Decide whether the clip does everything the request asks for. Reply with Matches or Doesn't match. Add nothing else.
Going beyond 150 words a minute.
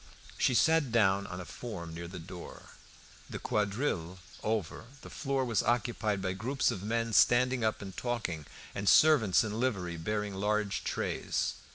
Matches